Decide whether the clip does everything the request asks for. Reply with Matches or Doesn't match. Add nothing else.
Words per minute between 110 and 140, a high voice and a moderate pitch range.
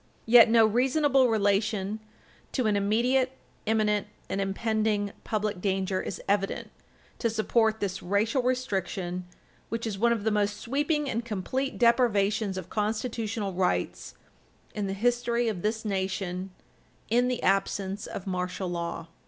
Matches